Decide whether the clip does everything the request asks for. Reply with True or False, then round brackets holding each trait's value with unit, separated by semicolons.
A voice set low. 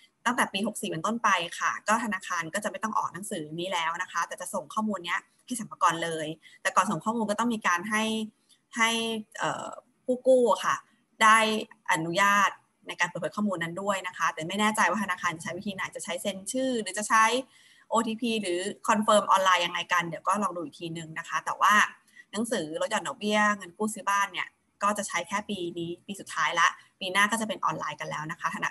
False (205 Hz)